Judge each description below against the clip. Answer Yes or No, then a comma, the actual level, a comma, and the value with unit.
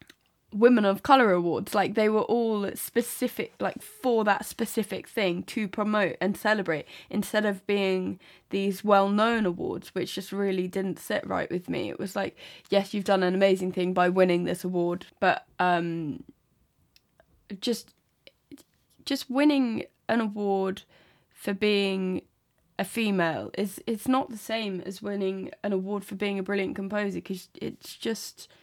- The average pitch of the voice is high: Yes, high, 200 Hz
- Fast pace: No, average, 155 wpm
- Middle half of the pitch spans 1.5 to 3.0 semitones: Yes, average, 2.7 semitones